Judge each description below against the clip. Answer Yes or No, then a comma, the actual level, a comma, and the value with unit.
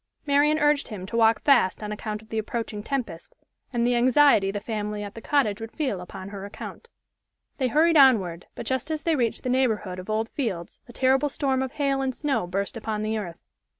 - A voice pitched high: Yes, high, 230 Hz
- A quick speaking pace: Yes, fast, 215 wpm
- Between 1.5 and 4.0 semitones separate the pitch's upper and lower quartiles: No, average, 4.6 semitones